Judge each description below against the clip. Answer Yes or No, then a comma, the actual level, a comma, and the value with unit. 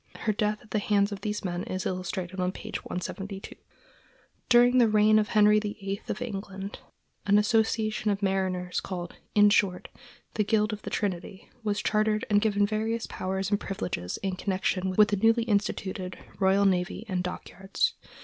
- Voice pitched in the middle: No, high, 205 Hz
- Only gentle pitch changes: Yes, narrow, 2.0 semitones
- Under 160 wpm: No, average, 170 wpm